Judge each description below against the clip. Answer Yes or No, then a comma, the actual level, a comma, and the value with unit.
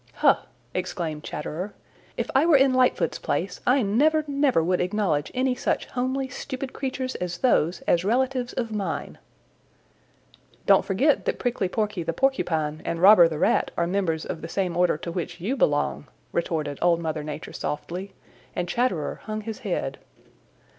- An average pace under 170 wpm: Yes, average, 160 wpm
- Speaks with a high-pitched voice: Yes, high, 195 Hz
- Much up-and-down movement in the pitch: Yes, wide, 7.2 semitones